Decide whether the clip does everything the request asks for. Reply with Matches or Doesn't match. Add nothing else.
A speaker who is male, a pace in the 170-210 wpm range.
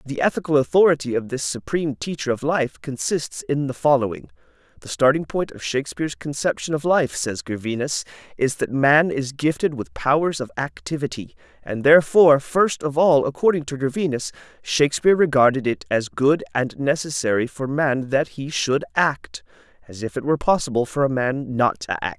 Matches